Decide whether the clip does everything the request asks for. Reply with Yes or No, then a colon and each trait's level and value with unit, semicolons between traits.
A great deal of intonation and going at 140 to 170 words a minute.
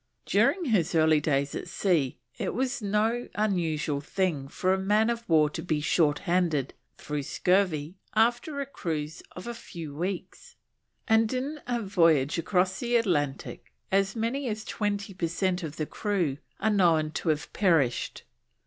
Yes: wide, 5.7 semitones; average, 160 wpm